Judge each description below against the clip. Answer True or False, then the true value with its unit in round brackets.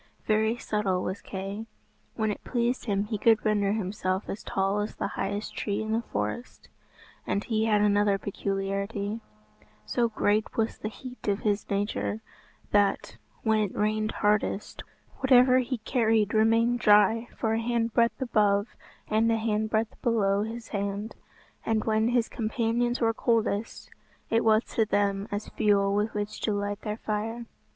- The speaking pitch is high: True (215 Hz)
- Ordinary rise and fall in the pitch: False (1.9 semitones)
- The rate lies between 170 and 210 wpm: False (155 wpm)